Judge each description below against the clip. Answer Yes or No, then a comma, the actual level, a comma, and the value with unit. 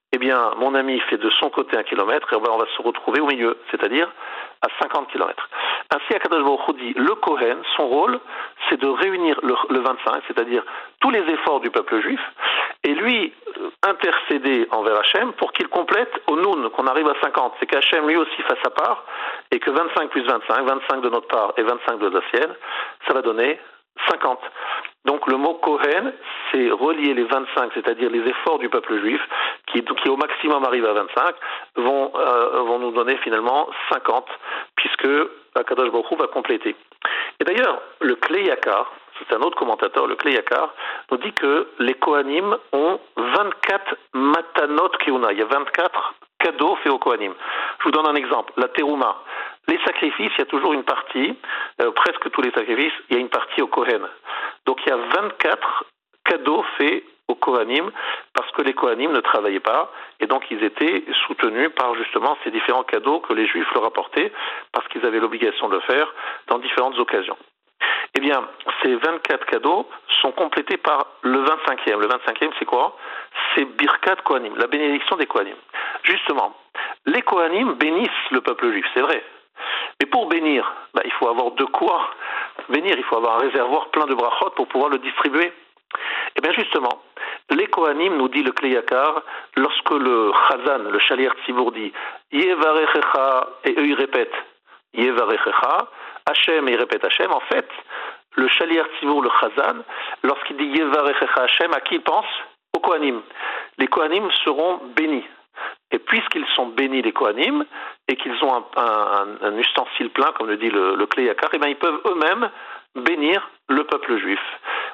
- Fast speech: No, average, 180 wpm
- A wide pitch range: Yes, wide, 6.1 semitones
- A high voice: Yes, very high, 390 Hz